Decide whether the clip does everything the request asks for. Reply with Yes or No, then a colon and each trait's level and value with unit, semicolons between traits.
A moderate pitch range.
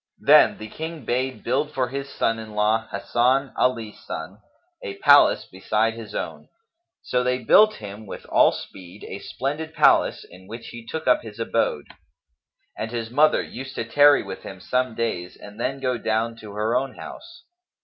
Yes: average, 3.7 semitones